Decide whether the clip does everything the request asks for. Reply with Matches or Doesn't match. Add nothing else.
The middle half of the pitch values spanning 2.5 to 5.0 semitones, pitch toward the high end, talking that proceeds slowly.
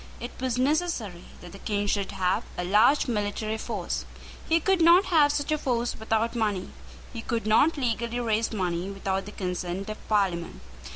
Doesn't match